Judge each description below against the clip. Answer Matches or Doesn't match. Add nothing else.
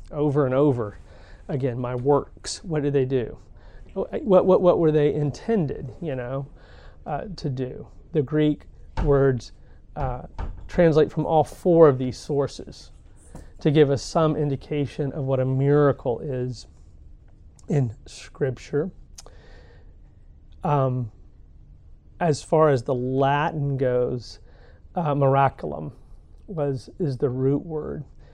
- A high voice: Doesn't match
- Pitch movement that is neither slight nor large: Doesn't match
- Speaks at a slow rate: Matches